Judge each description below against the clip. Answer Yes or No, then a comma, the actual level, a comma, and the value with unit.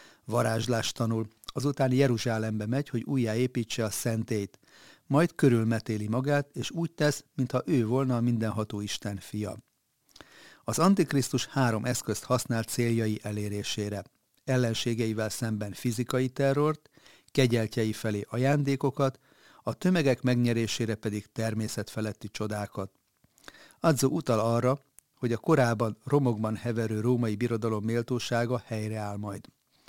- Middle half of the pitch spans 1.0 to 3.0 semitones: No, average, 3.4 semitones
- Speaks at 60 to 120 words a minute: Yes, average, 110 wpm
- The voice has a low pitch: Yes, low, 120 Hz